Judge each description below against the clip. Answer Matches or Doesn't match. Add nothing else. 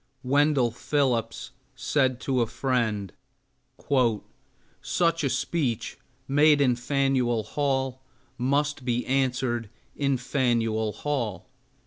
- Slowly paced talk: Matches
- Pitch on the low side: Matches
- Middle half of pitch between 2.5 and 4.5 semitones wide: Matches